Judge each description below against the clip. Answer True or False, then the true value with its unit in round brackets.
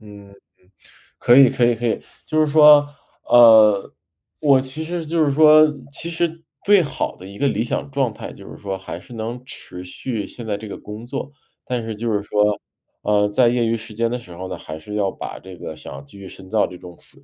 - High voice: False (115 Hz)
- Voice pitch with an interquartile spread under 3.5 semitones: False (5.2 semitones)